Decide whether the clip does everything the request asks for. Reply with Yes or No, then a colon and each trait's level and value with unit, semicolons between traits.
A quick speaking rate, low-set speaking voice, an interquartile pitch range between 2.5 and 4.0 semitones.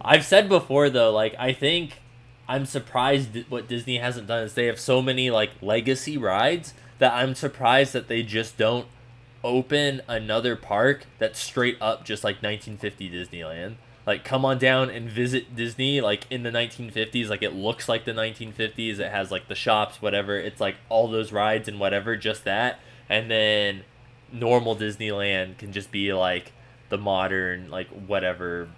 No: average, 170 wpm; low, 115 Hz; average, 3.2 semitones